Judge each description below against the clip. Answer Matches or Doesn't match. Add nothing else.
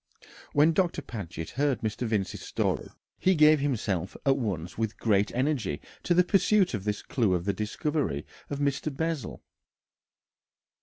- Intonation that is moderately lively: Doesn't match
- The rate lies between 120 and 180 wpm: Matches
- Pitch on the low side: Matches